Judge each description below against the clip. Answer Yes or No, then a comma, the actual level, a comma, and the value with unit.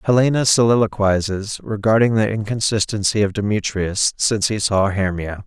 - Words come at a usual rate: No, slow, 120 wpm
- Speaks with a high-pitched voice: No, low, 105 Hz